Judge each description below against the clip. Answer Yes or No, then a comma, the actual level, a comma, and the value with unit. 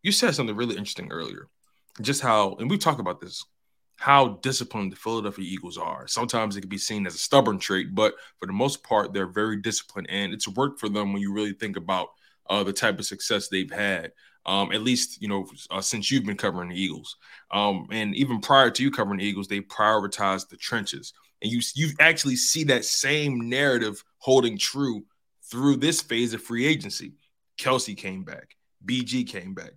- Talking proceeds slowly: No, average, 200 wpm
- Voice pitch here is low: Yes, low, 110 Hz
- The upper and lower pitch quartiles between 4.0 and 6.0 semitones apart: Yes, average, 4.7 semitones